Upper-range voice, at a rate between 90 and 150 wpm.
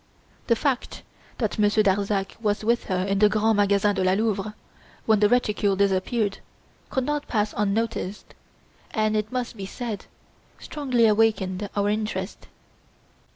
Yes: high, 210 Hz; average, 145 wpm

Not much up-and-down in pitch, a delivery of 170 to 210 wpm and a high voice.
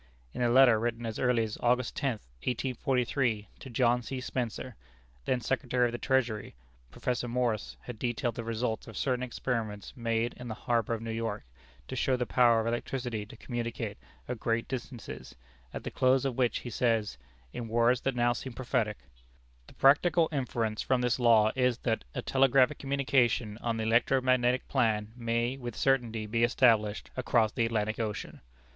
No: narrow, 2.0 semitones; average, 175 wpm; low, 120 Hz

